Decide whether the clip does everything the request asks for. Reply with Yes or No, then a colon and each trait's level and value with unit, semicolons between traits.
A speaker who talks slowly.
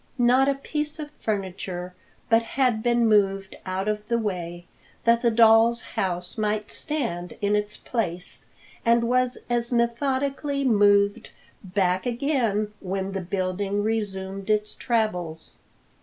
Yes: slow, 130 wpm